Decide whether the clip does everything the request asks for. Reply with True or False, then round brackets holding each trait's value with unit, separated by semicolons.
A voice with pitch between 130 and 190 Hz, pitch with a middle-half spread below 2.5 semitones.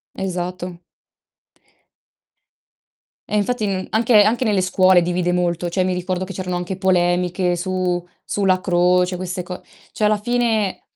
True (185 Hz; 1.9 semitones)